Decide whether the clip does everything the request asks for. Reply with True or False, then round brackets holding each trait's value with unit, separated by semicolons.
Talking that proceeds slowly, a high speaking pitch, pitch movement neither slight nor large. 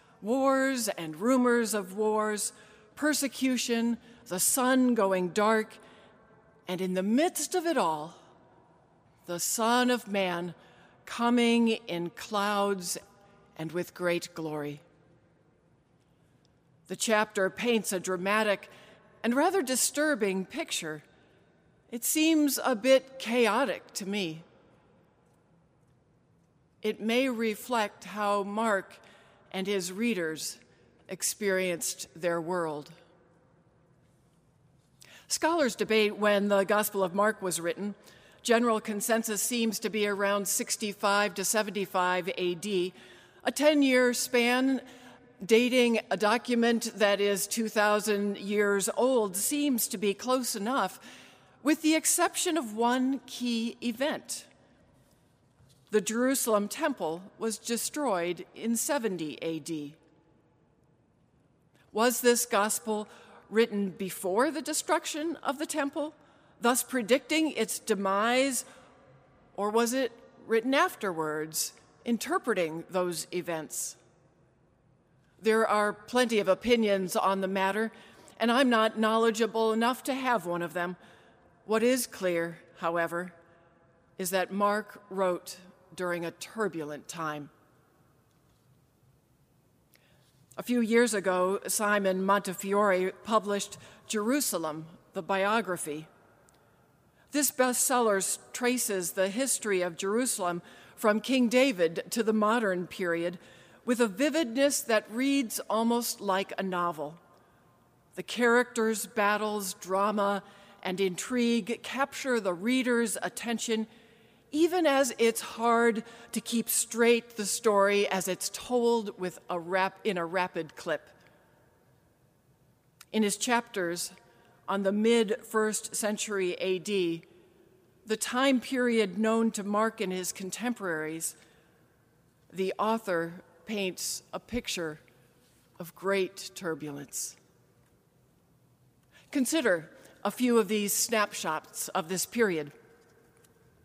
True (105 wpm; 205 Hz; 4.9 semitones)